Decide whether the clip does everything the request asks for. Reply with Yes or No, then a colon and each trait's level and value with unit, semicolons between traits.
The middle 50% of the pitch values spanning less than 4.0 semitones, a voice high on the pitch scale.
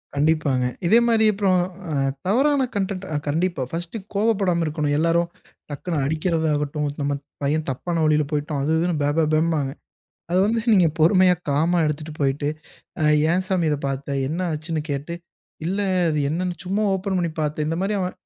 No: average, 3.6 semitones; medium, 165 Hz